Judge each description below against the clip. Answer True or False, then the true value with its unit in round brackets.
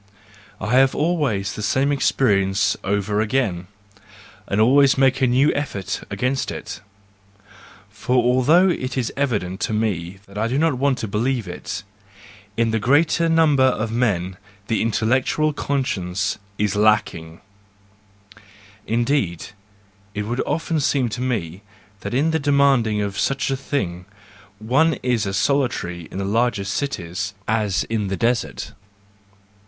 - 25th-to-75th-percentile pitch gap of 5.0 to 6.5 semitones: True (5.4 semitones)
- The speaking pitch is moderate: False (115 Hz)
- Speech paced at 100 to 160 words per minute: True (135 wpm)